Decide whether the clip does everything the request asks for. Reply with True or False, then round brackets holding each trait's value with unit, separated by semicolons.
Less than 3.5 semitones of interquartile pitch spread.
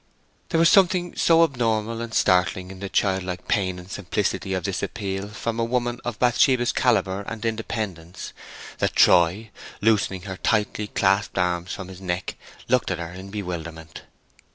False (3.9 semitones)